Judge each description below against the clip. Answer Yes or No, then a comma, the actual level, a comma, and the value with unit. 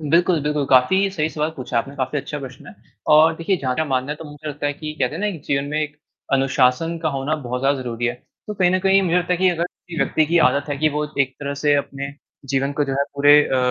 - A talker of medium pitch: Yes, medium, 145 Hz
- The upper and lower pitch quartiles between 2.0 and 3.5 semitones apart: Yes, average, 3.1 semitones